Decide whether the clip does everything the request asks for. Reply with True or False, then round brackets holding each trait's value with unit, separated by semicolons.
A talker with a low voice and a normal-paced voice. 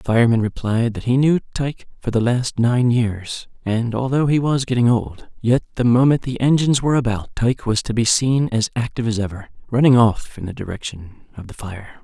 False (120 Hz; 210 wpm)